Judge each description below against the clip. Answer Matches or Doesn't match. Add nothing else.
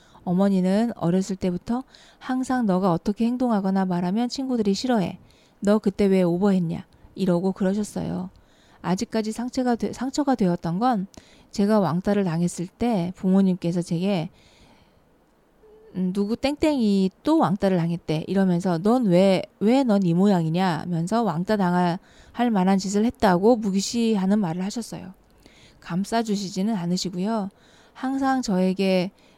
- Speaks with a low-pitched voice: Doesn't match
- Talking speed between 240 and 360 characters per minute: Matches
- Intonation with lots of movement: Doesn't match